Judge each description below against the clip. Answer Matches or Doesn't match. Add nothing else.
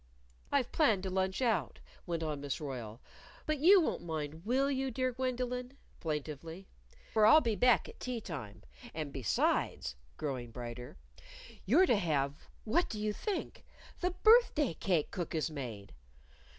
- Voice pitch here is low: Doesn't match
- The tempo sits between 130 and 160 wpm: Matches